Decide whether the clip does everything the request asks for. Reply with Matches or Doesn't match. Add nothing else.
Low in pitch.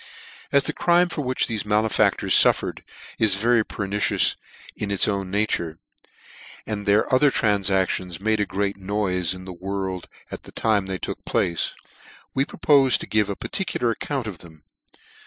Matches